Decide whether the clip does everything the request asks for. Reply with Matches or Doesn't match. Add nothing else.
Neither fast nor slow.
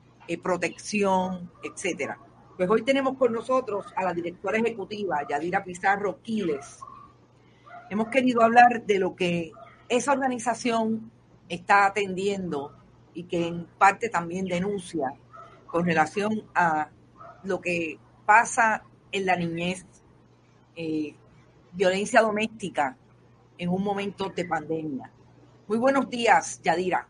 Doesn't match